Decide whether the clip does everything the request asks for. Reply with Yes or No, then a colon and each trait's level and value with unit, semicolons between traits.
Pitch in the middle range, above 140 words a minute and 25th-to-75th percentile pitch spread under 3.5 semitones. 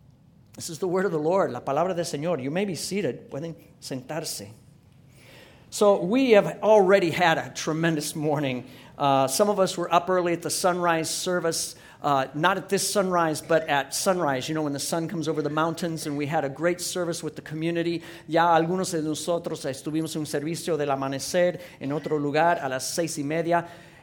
Yes: medium, 165 Hz; average, 200 wpm; average, 3.0 semitones